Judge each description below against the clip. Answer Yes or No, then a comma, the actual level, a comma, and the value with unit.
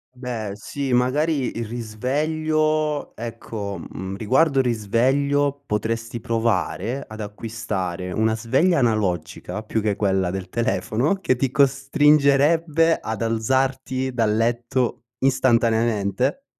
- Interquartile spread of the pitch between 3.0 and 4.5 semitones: Yes, average, 4.2 semitones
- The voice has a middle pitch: No, low, 120 Hz